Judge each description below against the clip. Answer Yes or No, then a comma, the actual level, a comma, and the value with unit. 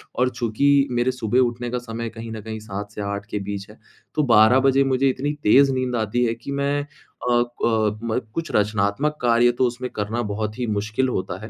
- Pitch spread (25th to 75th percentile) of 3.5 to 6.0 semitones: No, average, 3.1 semitones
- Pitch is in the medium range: No, low, 115 Hz